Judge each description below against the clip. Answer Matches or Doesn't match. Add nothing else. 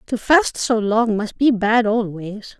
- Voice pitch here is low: Doesn't match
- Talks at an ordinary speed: Matches